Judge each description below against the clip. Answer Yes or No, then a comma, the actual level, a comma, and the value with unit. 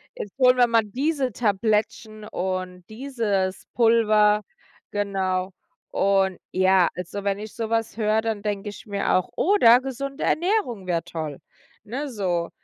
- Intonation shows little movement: No, average, 3.6 semitones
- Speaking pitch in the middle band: No, high, 210 Hz